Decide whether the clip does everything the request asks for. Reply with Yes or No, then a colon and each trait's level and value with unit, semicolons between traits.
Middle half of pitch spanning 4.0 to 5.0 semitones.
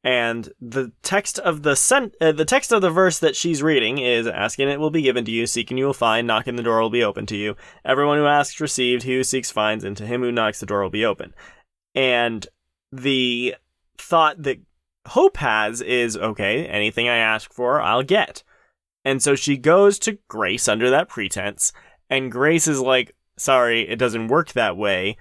Yes: average, 4.5 semitones